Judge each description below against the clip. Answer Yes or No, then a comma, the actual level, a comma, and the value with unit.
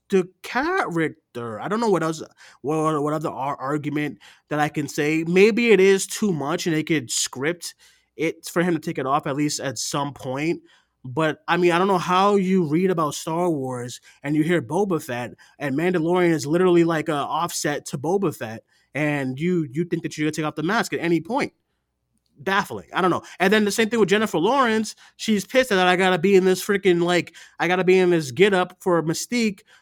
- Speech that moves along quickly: Yes, fast, 215 wpm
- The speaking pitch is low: No, medium, 170 Hz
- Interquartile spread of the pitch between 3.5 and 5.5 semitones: Yes, average, 3.8 semitones